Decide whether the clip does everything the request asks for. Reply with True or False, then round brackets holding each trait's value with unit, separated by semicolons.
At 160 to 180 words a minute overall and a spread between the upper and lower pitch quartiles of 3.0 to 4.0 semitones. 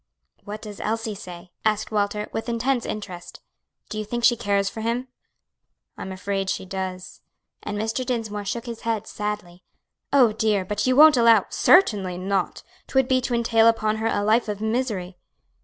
False (175 wpm; 2.6 semitones)